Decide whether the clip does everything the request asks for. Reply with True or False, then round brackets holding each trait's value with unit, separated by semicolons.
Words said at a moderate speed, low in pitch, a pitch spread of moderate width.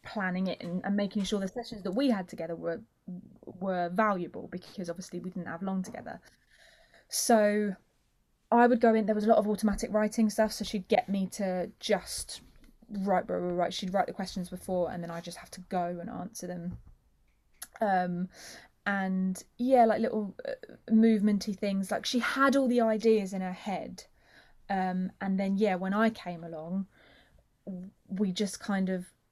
False (180 wpm; 195 Hz; 3.1 semitones)